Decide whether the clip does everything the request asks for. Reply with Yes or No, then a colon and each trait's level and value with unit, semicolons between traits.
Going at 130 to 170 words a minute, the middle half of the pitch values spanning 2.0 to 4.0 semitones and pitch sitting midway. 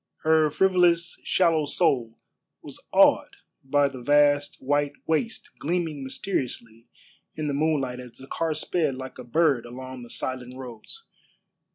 Yes: average, 140 wpm; average, 3.7 semitones; medium, 145 Hz